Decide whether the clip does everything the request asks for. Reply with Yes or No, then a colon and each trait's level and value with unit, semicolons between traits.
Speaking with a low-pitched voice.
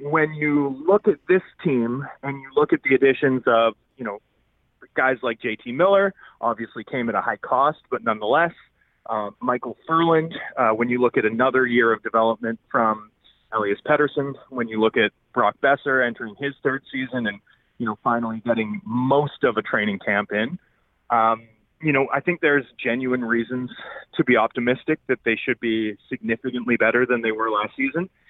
Yes: low, 125 Hz